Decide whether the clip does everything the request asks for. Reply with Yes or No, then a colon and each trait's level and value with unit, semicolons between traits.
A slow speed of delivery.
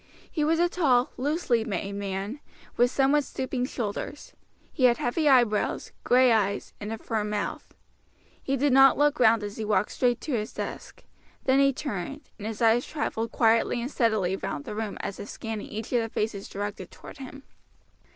No: average, 185 wpm